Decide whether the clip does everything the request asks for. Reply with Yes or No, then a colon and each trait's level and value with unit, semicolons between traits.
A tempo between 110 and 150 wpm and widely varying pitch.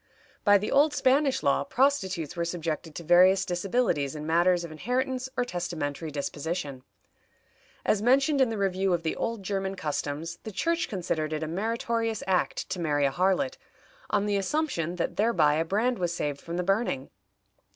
No: average, 170 wpm; wide, 5.9 semitones